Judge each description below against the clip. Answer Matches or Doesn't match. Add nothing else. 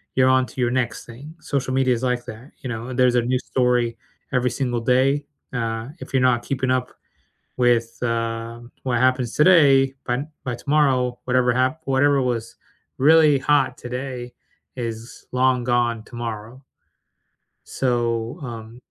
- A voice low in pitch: Matches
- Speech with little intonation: Matches